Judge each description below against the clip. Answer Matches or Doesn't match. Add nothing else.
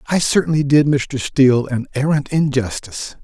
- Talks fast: Doesn't match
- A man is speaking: Matches